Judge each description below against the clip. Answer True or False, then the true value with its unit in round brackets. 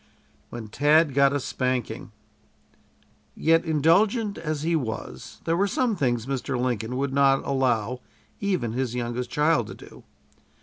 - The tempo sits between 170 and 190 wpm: False (140 wpm)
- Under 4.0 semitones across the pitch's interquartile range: False (4.8 semitones)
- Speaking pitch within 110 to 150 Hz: True (135 Hz)